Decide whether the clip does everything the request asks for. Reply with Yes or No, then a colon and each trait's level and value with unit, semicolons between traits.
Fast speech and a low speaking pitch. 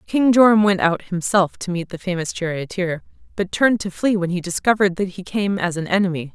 No: fast, 220 wpm; medium, 185 Hz